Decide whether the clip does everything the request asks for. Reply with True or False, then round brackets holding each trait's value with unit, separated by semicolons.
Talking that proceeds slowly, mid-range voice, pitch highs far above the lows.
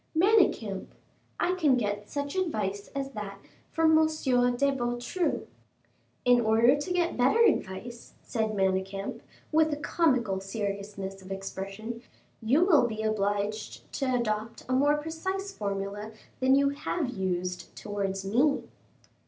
False (130 wpm; 235 Hz; 6.4 semitones)